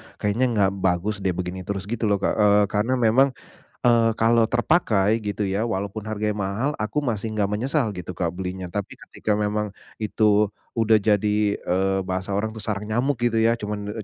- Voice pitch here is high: No, low, 105 Hz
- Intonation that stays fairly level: Yes, narrow, 2.3 semitones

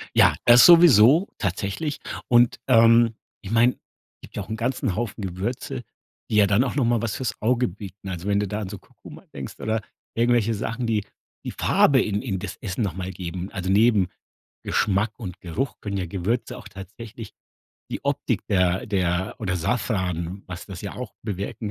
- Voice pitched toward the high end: No, low, 105 Hz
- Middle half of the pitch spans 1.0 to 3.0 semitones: No, average, 3.9 semitones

